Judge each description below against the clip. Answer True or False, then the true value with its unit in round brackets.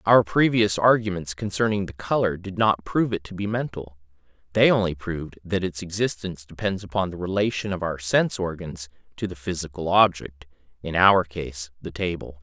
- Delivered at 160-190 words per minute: True (170 wpm)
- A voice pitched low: True (90 Hz)